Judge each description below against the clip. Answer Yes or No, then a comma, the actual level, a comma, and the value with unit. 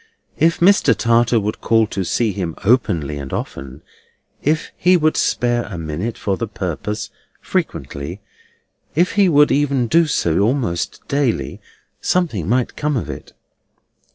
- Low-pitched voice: Yes, low, 115 Hz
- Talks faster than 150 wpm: No, average, 145 wpm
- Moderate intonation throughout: No, wide, 8.0 semitones